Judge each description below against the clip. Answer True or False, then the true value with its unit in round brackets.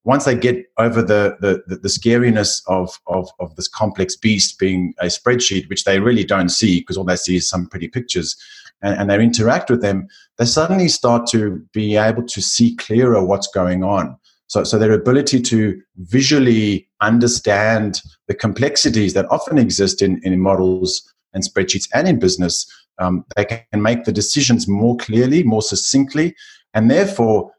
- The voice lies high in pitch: False (105 Hz)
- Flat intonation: False (3.7 semitones)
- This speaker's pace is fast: False (175 wpm)